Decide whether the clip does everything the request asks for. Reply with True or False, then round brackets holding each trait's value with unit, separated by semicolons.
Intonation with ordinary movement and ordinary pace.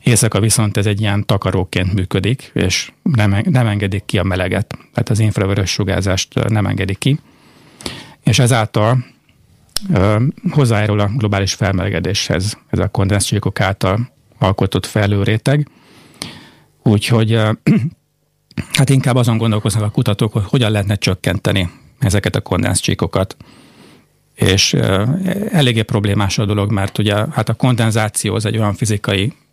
True (4.0 semitones; 130 wpm)